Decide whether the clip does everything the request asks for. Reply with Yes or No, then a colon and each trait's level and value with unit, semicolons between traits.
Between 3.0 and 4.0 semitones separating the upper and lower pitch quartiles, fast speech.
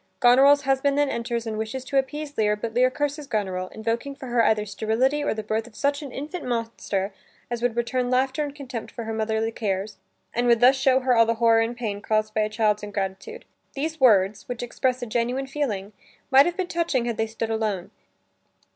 Yes: average, 3.6 semitones; fast, 210 wpm